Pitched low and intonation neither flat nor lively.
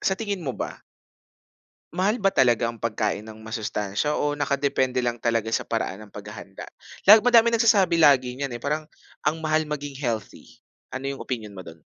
No: low, 130 Hz; wide, 5.8 semitones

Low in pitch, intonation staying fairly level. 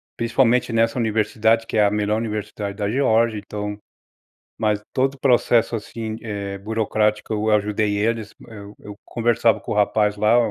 Yes: low, 110 Hz; narrow, 1.7 semitones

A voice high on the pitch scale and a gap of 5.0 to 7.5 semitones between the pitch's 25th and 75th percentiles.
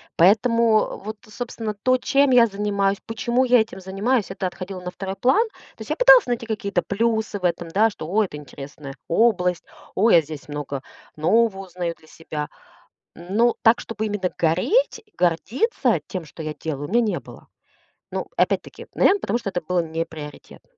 Yes: high, 200 Hz; average, 5.3 semitones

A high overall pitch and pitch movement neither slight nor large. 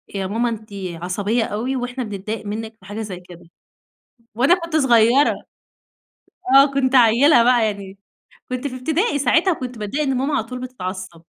Yes: high, 235 Hz; average, 4.3 semitones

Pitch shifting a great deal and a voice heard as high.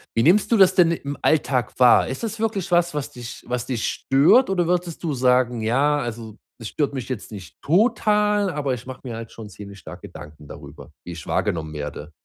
No: wide, 7.4 semitones; low, 130 Hz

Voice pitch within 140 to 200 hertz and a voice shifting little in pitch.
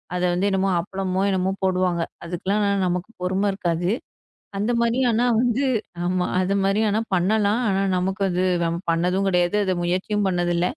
Yes: high, 190 Hz; narrow, 2.2 semitones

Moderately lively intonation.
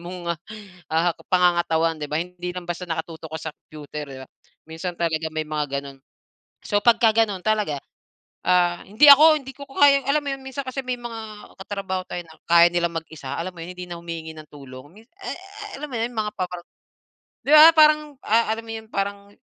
No: wide, 6.1 semitones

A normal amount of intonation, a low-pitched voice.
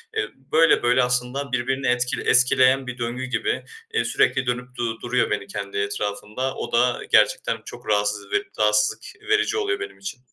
Yes: average, 3.6 semitones; low, 125 Hz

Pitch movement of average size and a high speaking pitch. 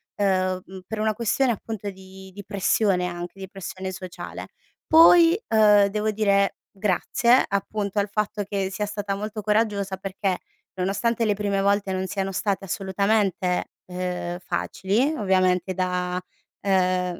No: narrow, 2.1 semitones; high, 195 Hz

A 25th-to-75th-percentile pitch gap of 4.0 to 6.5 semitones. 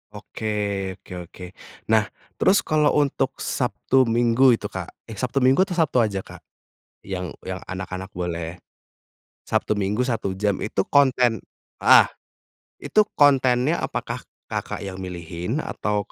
Yes: wide, 5.6 semitones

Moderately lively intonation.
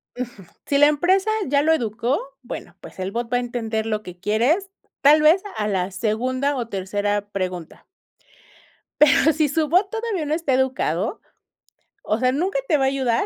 No: wide, 6.2 semitones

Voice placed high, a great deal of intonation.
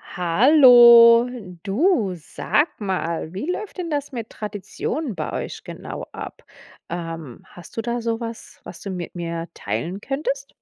Yes: high, 225 Hz; wide, 7.2 semitones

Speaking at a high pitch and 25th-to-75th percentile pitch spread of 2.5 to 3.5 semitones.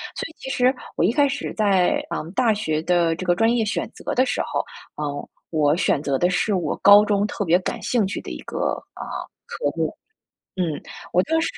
No: high, 200 Hz; wide, 5.5 semitones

